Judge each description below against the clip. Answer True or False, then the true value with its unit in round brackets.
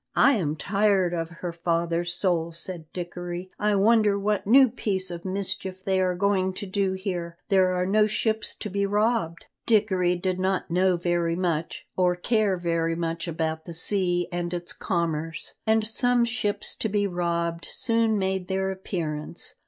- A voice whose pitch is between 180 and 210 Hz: True (185 Hz)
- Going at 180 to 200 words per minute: False (170 wpm)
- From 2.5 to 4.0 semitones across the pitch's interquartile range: True (2.9 semitones)